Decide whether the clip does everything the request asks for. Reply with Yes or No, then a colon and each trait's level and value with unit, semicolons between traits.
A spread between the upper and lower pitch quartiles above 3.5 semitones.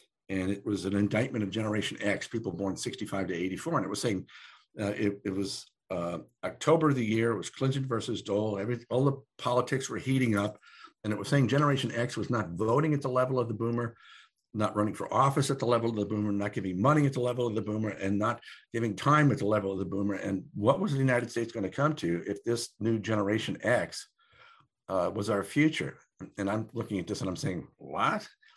Yes: average, 4.3 semitones